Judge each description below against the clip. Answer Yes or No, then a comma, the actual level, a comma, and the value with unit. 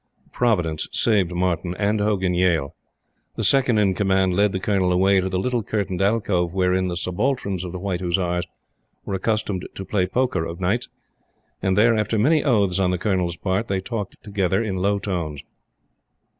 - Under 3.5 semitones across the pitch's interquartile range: Yes, narrow, 2.5 semitones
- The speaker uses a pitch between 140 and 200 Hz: No, very low, 95 Hz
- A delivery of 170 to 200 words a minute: Yes, average, 175 wpm